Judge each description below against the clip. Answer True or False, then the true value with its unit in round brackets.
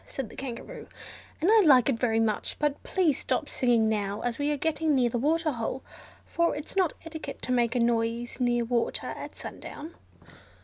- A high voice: True (255 Hz)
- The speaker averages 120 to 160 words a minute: False (185 wpm)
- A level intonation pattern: False (4.7 semitones)